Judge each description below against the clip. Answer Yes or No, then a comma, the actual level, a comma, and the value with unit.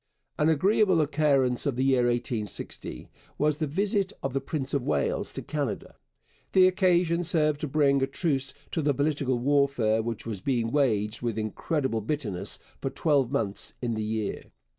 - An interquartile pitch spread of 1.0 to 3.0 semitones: No, average, 4.4 semitones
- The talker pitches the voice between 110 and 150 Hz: Yes, medium, 140 Hz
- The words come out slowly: No, average, 165 wpm